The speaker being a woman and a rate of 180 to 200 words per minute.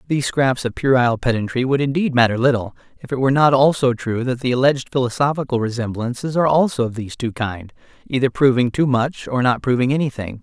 No: male; average, 195 wpm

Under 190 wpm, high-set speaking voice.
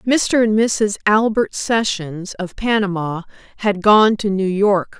Yes: average, 145 wpm; high, 205 Hz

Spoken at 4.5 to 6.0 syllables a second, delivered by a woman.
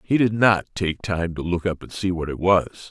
No: 4.8 syllables/s; male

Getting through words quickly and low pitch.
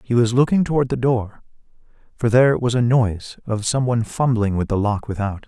No: average, 195 wpm; low, 120 Hz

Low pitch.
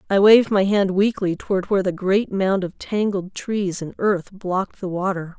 No: high, 195 Hz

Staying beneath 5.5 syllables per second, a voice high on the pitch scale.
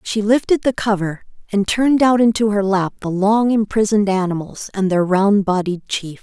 Yes: 5.0 syllables/s; high, 205 Hz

